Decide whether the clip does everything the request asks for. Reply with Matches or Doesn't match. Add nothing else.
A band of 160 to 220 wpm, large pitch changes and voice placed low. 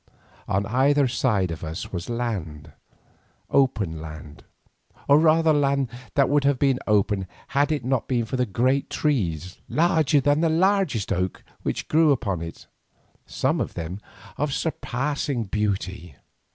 Doesn't match